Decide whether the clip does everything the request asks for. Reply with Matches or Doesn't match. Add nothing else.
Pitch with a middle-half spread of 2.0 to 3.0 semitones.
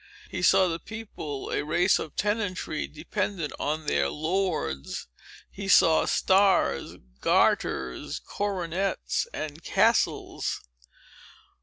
Doesn't match